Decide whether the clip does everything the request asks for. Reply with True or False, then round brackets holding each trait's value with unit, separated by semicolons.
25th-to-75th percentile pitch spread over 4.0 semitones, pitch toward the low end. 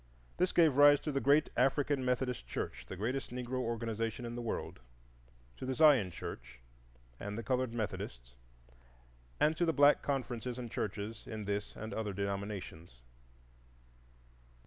True (4.7 semitones; 120 Hz)